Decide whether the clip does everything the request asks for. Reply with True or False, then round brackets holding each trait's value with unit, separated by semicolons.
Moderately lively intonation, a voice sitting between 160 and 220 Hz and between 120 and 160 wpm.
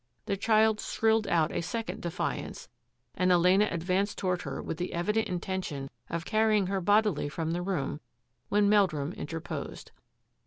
True (3.8 semitones; 185 Hz; 155 wpm)